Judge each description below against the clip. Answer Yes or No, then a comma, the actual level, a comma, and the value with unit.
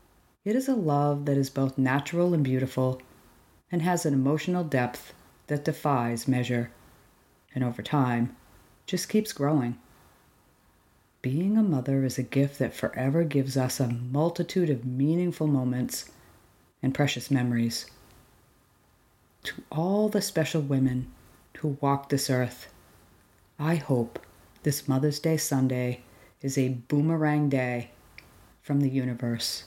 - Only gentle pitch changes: No, average, 3.4 semitones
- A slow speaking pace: Yes, slow, 130 wpm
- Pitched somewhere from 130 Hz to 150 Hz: Yes, low, 135 Hz